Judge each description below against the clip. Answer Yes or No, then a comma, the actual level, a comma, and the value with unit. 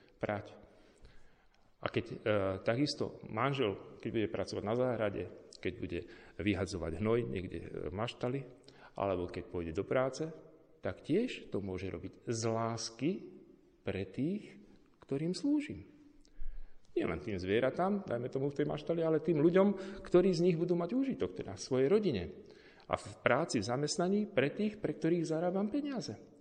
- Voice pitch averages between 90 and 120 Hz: No, low, 135 Hz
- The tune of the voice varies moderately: No, wide, 8.9 semitones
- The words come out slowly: No, average, 150 wpm